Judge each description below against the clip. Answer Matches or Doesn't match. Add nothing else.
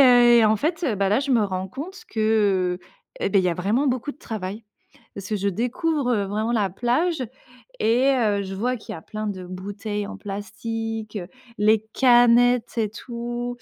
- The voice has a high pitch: Matches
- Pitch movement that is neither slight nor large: Matches